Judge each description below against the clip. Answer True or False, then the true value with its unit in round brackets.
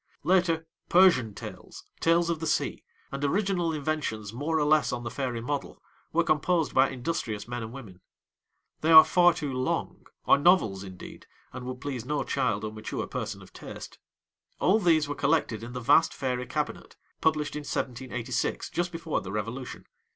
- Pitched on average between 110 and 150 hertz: True (140 Hz)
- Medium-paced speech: True (175 wpm)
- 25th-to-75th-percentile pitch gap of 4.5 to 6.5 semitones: True (5.2 semitones)